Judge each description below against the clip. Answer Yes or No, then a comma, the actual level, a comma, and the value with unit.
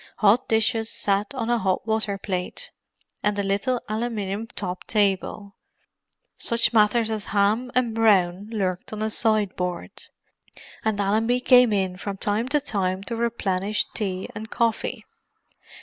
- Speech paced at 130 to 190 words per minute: Yes, average, 140 wpm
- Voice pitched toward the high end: Yes, high, 210 Hz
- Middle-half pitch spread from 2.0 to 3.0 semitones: Yes, narrow, 2.5 semitones